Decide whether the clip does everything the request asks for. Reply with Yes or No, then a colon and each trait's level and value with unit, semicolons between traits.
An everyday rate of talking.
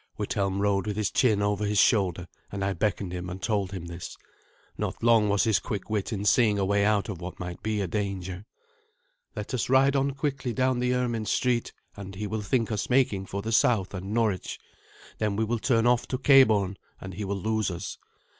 No: fast, 210 wpm